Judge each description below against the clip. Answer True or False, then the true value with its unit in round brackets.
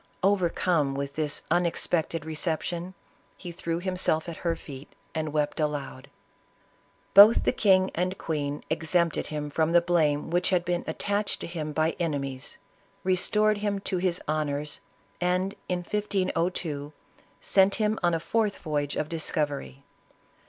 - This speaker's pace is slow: False (150 wpm)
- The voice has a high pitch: False (170 Hz)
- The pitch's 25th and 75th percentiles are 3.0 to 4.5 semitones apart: True (3.5 semitones)